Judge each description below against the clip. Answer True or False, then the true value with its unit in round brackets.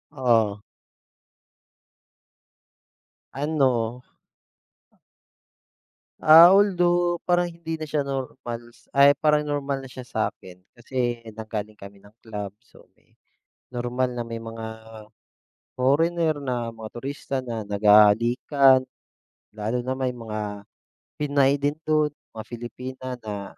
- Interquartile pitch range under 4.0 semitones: False (4.3 semitones)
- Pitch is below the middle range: True (125 Hz)